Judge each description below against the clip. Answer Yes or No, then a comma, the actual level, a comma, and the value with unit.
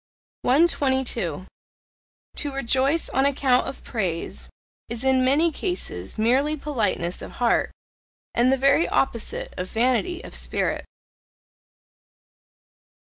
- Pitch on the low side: No, very high, 260 Hz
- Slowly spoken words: Yes, slow, 105 wpm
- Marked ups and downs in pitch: No, average, 3.4 semitones